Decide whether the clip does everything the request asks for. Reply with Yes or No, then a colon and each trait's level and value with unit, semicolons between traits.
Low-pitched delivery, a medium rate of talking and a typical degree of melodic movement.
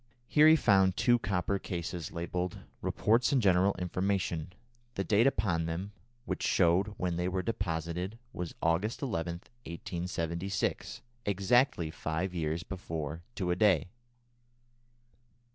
No: very low, 90 Hz; slow, 125 wpm; average, 3.1 semitones